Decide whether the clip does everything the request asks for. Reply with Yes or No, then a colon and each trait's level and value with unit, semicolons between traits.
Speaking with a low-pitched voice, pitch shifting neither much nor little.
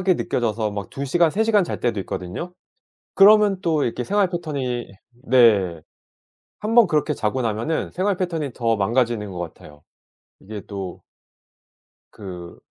No: low, 125 Hz; wide, 9.0 semitones